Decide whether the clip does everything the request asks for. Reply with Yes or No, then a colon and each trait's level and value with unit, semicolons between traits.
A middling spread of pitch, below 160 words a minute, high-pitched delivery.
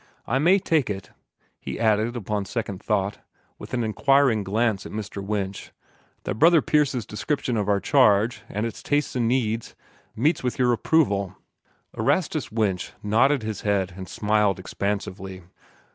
No: average, 3.8 semitones; average, 150 wpm; low, 110 Hz